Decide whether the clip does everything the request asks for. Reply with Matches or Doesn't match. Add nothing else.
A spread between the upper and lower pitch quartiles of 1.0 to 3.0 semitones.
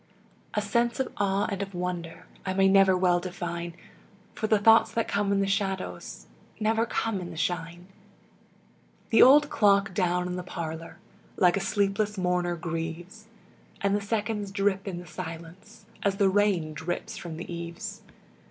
Matches